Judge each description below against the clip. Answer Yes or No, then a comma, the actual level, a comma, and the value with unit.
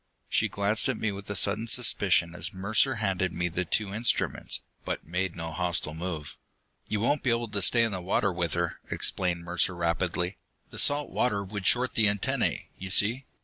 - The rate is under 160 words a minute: No, average, 190 wpm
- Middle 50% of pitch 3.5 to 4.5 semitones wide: Yes, average, 3.8 semitones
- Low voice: Yes, low, 100 Hz